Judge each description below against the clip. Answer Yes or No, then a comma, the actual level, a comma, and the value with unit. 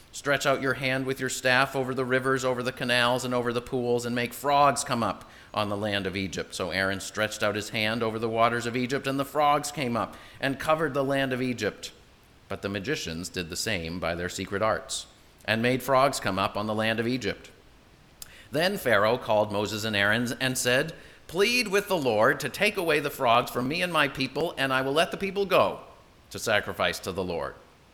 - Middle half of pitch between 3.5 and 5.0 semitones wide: Yes, average, 4.0 semitones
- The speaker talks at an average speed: No, fast, 220 wpm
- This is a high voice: No, low, 125 Hz